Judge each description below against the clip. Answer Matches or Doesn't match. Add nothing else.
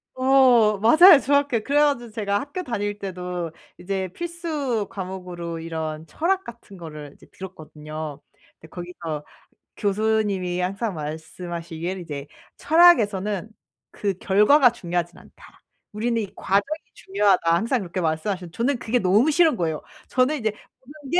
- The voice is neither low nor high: Doesn't match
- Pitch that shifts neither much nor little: Doesn't match